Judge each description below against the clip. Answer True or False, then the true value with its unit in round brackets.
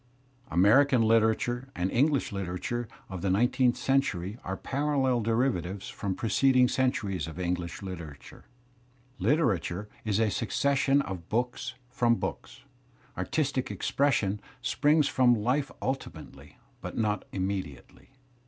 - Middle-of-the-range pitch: False (115 Hz)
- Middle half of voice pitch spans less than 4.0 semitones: False (5.5 semitones)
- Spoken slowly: True (120 wpm)